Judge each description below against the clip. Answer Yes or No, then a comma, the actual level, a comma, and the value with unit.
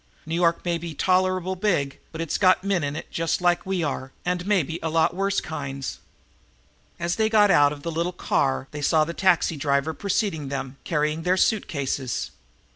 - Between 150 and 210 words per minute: Yes, average, 200 wpm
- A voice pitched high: No, medium, 165 Hz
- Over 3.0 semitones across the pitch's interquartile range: Yes, average, 4.0 semitones